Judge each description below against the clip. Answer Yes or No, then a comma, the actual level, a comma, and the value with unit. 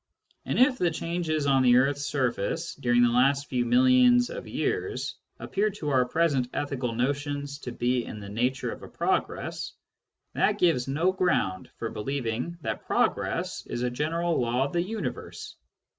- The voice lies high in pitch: No, medium, 140 Hz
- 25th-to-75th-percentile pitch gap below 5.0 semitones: No, wide, 5.4 semitones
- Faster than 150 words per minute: Yes, average, 165 wpm